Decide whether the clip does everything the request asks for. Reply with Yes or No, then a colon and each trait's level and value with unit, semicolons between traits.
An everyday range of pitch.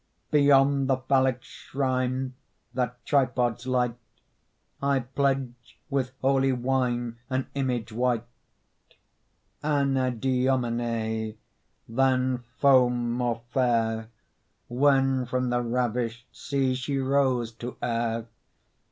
No: narrow, 1.9 semitones